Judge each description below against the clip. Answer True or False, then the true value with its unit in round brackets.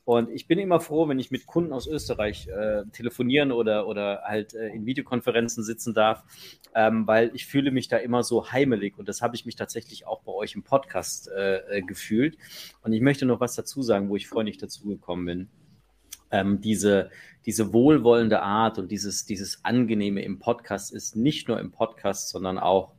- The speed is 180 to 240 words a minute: True (190 wpm)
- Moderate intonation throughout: True (3.0 semitones)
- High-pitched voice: False (110 Hz)